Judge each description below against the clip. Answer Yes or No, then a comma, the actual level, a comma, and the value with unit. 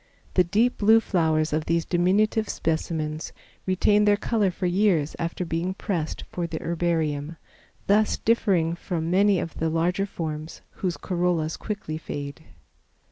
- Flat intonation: No, average, 3.7 semitones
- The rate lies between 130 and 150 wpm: Yes, average, 140 wpm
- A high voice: No, medium, 175 Hz